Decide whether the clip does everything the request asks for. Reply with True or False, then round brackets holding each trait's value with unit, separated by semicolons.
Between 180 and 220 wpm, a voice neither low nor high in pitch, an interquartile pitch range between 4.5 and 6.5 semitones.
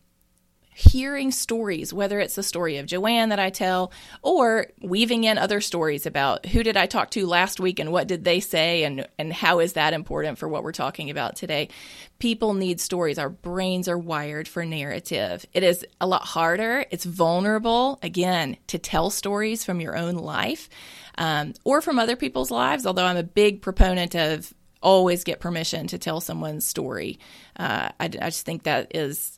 False (185 wpm; 180 Hz; 3.7 semitones)